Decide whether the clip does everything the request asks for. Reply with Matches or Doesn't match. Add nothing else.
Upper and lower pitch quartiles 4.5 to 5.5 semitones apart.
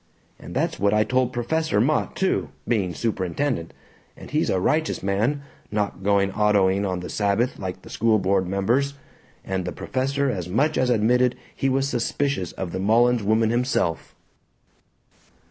Matches